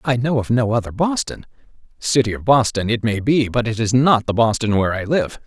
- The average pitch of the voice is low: Yes, low, 120 Hz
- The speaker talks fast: Yes, fast, 230 wpm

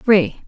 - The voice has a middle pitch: No, high, 210 Hz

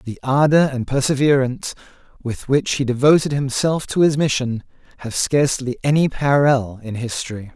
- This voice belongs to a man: Yes, male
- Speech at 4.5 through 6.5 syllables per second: Yes, 5.3 syllables/s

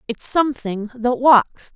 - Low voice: No, high, 245 Hz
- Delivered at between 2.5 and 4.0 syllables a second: Yes, 3.9 syllables/s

